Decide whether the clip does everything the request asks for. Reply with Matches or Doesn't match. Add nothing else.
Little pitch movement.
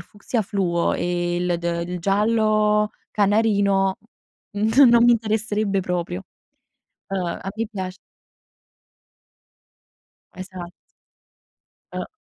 Doesn't match